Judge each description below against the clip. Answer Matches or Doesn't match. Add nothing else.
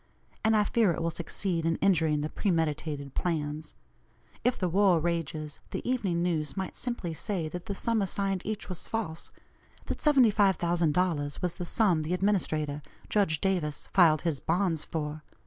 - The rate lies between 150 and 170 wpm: Matches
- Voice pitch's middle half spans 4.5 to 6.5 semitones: Doesn't match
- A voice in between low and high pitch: Matches